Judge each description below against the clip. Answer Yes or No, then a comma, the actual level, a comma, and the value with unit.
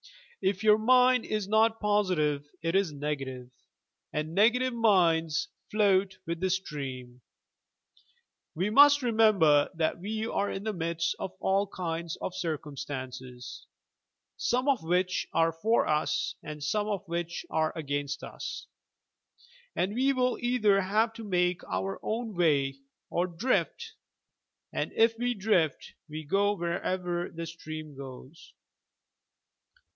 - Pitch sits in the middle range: Yes, medium, 180 Hz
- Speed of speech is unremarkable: No, slow, 130 wpm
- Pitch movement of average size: No, wide, 5.7 semitones